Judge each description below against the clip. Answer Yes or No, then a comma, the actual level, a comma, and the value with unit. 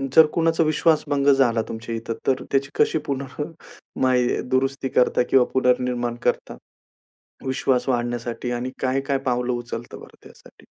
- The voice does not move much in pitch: Yes, narrow, 2.0 semitones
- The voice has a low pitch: Yes, low, 130 Hz